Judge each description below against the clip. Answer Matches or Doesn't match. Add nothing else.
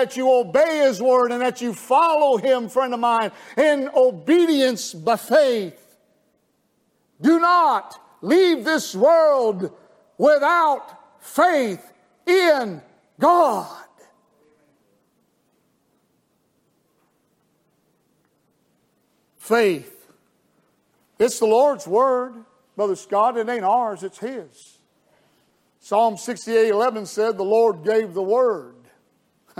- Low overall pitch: Doesn't match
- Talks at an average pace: Doesn't match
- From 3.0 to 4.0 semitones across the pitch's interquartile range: Doesn't match